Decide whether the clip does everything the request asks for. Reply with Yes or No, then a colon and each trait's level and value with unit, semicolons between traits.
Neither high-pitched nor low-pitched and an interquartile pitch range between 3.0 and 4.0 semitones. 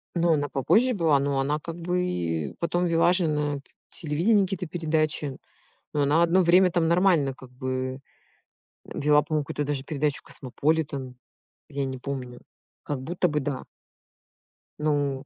Yes: medium, 150 Hz; average, 3.6 semitones